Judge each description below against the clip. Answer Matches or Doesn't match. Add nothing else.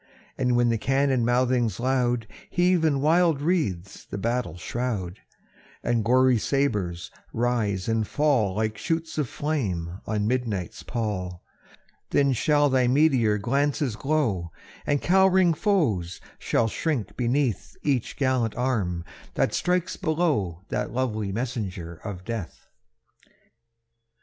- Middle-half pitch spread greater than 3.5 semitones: Matches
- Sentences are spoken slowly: Matches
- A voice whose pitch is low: Matches